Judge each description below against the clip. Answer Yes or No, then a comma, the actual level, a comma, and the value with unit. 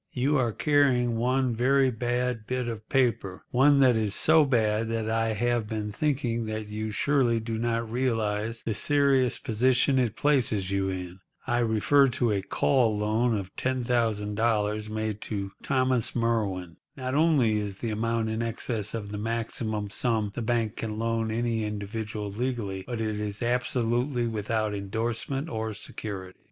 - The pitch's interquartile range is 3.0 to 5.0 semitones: No, narrow, 2.6 semitones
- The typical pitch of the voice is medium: No, low, 115 Hz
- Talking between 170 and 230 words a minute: No, average, 155 wpm